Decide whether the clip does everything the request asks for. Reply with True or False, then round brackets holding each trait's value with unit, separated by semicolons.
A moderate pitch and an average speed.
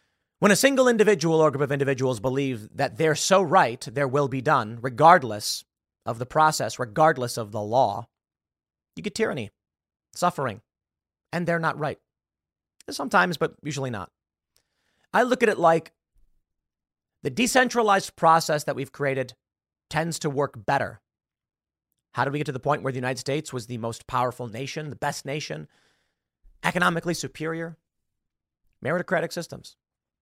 True (145 Hz; 150 wpm)